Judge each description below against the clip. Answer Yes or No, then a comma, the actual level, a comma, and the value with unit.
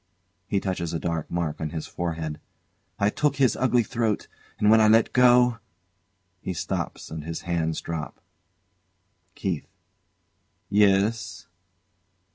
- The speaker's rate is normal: No, slow, 125 wpm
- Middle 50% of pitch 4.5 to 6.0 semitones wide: Yes, wide, 5.5 semitones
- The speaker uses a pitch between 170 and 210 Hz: No, very low, 95 Hz